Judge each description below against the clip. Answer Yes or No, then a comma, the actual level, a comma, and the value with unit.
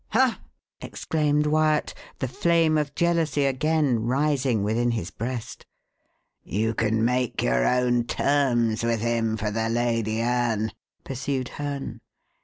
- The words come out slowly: Yes, slow, 125 wpm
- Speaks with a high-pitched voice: No, low, 125 Hz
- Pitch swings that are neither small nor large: Yes, average, 4.4 semitones